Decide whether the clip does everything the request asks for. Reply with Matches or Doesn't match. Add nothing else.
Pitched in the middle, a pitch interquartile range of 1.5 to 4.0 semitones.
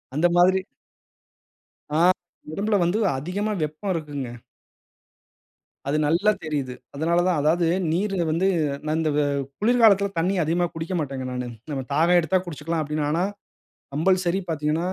Matches